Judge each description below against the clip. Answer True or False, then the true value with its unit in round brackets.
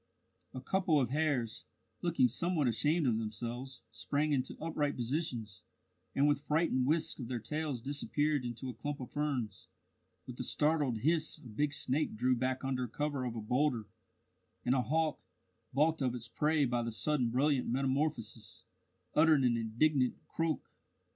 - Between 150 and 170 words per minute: True (160 wpm)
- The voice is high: False (135 Hz)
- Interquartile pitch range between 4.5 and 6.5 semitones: False (3.9 semitones)